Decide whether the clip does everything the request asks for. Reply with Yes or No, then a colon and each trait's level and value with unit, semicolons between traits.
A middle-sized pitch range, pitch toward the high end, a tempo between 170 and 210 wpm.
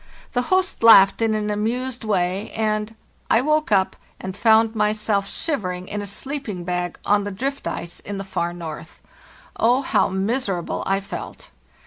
No: average, 3.4 semitones; high, 210 Hz; average, 155 wpm